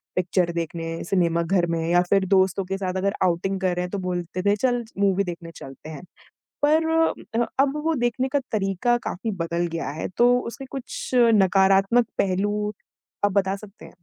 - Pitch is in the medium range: No, high, 195 Hz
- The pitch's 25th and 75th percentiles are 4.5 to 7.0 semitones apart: No, average, 3.6 semitones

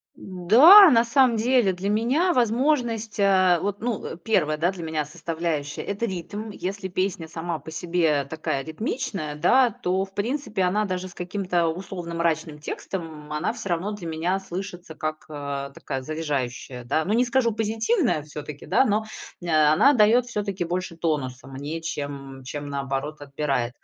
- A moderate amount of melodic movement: No, wide, 5.7 semitones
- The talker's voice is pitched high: No, medium, 175 Hz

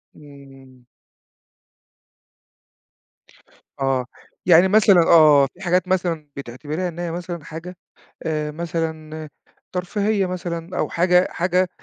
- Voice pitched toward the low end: No, medium, 170 Hz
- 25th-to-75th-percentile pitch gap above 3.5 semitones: No, average, 3.1 semitones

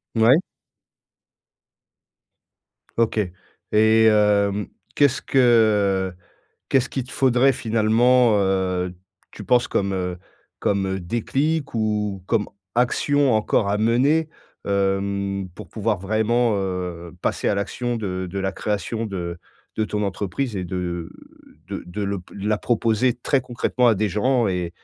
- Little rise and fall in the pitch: No, average, 3.7 semitones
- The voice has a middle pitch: No, low, 105 Hz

